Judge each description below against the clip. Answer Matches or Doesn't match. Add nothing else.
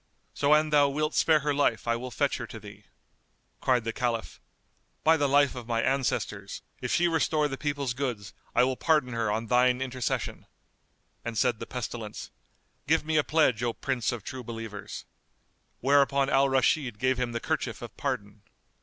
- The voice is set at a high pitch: Doesn't match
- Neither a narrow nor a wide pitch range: Matches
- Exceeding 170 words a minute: Matches